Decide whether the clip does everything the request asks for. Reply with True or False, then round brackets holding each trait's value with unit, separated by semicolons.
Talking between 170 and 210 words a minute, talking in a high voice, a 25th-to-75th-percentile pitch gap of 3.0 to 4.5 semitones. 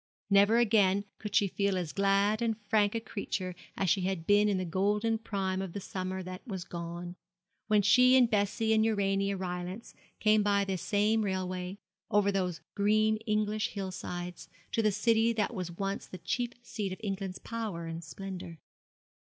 False (175 wpm; 200 Hz; 2.5 semitones)